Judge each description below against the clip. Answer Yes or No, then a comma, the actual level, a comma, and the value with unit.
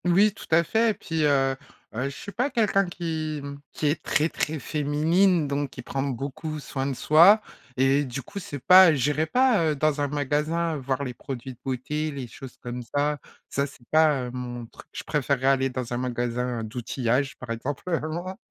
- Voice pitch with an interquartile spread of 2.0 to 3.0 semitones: No, average, 3.7 semitones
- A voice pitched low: No, medium, 145 Hz